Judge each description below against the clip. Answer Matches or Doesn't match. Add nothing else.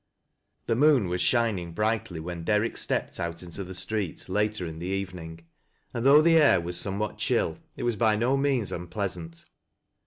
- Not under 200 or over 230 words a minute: Doesn't match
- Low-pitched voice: Matches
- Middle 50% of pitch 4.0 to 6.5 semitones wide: Matches